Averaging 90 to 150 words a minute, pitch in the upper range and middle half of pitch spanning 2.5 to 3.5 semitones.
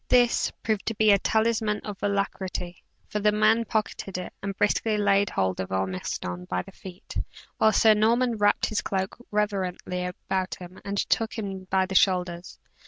No: average, 170 wpm; high, 200 Hz; average, 2.8 semitones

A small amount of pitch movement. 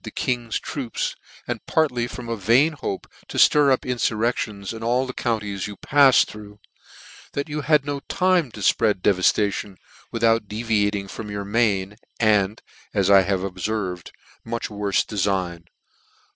No: average, 3.6 semitones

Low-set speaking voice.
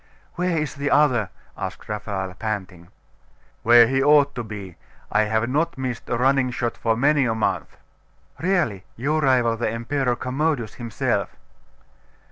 Yes: low, 120 Hz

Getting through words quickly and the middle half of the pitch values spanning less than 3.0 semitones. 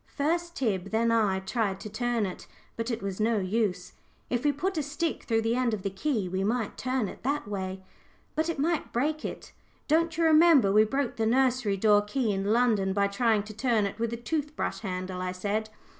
No: fast, 220 wpm; average, 5.2 semitones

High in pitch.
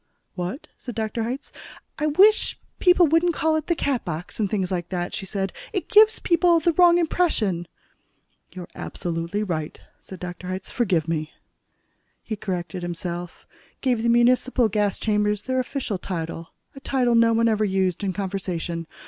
Yes: high, 210 Hz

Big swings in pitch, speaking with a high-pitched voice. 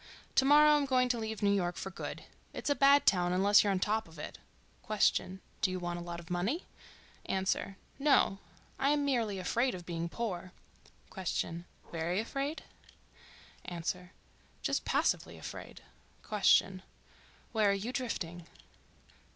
Yes: wide, 5.8 semitones; high, 195 Hz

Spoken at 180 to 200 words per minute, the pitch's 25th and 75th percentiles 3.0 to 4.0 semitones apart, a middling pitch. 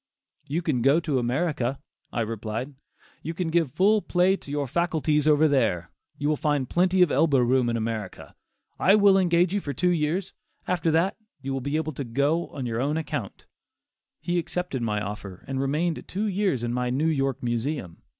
No: average, 190 wpm; wide, 5.5 semitones; medium, 145 Hz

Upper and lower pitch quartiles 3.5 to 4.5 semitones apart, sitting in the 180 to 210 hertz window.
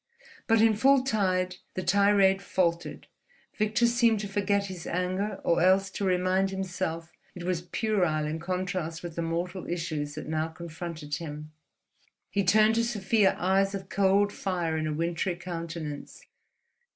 No: average, 3.0 semitones; medium, 185 Hz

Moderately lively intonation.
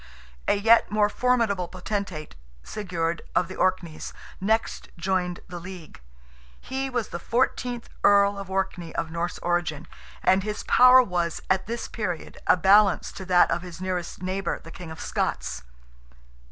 Yes: average, 3.2 semitones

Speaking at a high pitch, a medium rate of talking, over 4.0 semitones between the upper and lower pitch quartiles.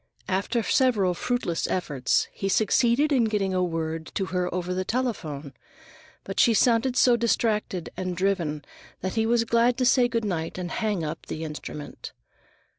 Yes: high, 195 Hz; average, 165 wpm; average, 5.1 semitones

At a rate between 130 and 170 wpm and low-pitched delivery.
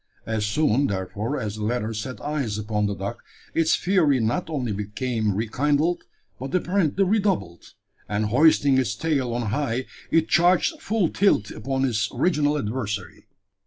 Yes: average, 150 wpm; low, 130 Hz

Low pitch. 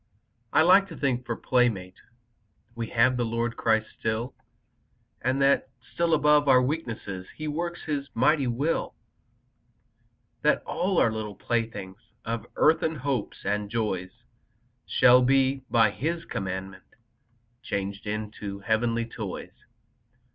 Yes: low, 120 Hz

